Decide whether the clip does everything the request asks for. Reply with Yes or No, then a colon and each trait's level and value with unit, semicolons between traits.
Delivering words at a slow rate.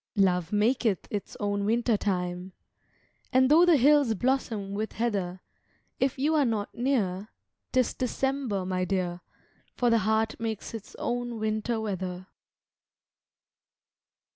Yes: slow, 125 wpm